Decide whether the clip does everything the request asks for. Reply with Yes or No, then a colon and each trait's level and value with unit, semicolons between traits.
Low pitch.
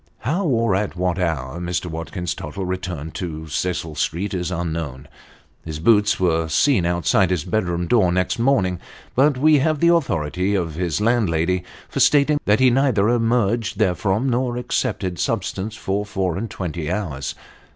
Yes: very low, 95 Hz